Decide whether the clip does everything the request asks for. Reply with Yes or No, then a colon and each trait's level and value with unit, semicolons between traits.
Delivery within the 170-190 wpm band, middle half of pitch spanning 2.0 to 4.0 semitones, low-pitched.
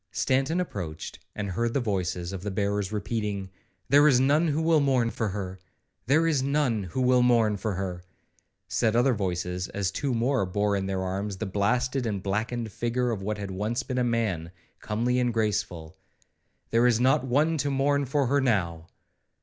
No: average, 180 wpm; average, 4.8 semitones; low, 115 Hz